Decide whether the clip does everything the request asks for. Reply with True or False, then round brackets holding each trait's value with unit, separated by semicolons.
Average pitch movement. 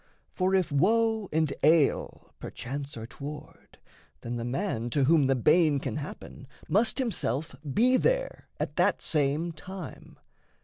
False (5.7 semitones)